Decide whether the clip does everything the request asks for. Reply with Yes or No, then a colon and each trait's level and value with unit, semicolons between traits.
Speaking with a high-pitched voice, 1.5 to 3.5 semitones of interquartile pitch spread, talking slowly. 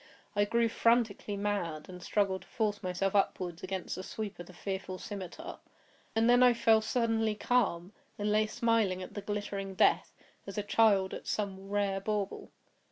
No: high, 205 Hz; narrow, 2.5 semitones; average, 170 wpm